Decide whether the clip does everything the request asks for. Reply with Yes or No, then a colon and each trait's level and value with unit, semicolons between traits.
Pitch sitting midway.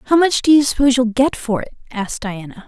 No: high, 245 Hz